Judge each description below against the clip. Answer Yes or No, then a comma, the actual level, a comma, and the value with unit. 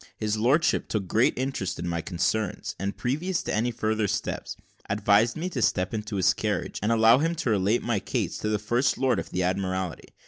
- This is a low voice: Yes, low, 110 Hz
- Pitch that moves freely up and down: No, average, 3.8 semitones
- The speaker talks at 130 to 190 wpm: No, fast, 205 wpm